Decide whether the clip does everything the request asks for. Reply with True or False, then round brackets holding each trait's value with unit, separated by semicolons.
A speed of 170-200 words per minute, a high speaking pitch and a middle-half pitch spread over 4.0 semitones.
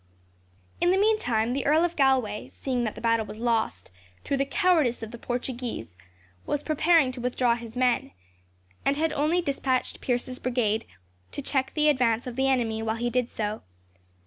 False (175 wpm; 250 Hz; 3.4 semitones)